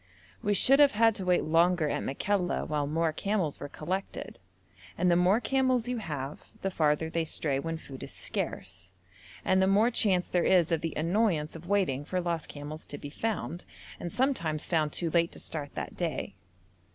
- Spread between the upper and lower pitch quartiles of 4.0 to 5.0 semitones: Yes, average, 4.3 semitones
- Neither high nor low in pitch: Yes, medium, 170 Hz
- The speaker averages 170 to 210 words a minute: Yes, average, 190 wpm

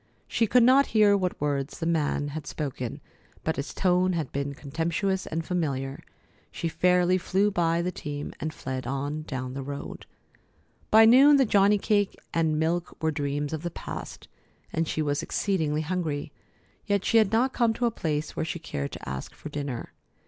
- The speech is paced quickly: No, average, 185 wpm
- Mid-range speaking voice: Yes, medium, 160 Hz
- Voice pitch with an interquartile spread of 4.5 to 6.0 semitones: Yes, average, 4.9 semitones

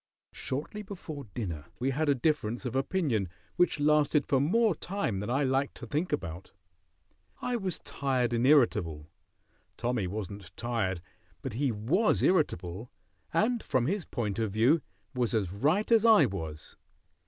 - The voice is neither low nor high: No, low, 130 Hz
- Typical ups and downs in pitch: No, wide, 6.9 semitones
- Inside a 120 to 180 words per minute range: Yes, average, 155 wpm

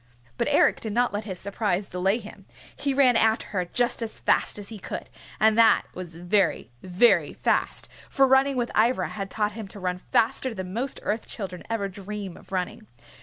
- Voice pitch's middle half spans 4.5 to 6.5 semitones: No, average, 3.6 semitones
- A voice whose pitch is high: Yes, high, 210 Hz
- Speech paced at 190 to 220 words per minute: Yes, average, 195 wpm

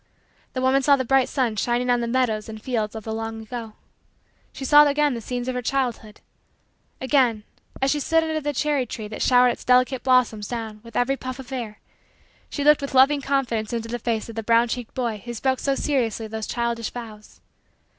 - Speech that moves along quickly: Yes, fast, 210 wpm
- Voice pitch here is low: No, high, 245 Hz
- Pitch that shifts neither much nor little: Yes, average, 3.1 semitones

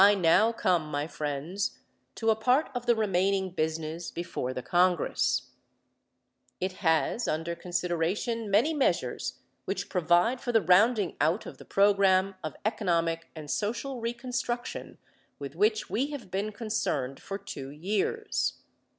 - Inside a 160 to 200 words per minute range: No, average, 140 wpm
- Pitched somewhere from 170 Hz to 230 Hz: Yes, high, 190 Hz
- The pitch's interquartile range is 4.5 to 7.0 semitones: Yes, average, 5.3 semitones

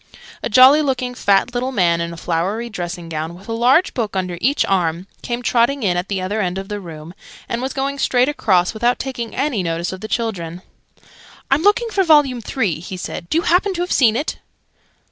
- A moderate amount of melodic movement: No, wide, 6.6 semitones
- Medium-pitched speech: No, high, 220 Hz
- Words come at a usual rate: No, fast, 215 wpm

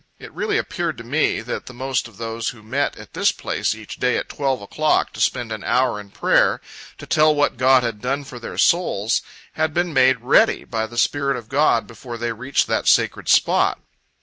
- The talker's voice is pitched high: No, low, 125 Hz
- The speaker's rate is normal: No, fast, 210 wpm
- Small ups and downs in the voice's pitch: No, average, 3.7 semitones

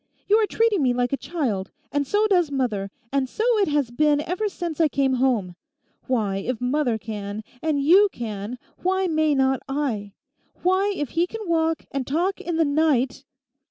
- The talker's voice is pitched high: Yes, very high, 285 Hz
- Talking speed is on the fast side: No, average, 185 wpm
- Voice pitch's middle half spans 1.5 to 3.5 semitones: No, wide, 5.6 semitones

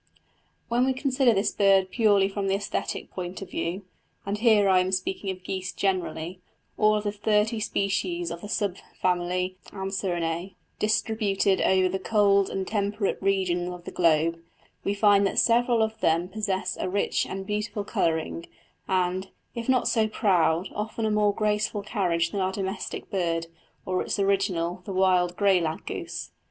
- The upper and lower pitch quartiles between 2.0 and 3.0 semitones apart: Yes, narrow, 2.4 semitones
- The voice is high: Yes, high, 195 Hz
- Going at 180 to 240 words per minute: No, average, 170 wpm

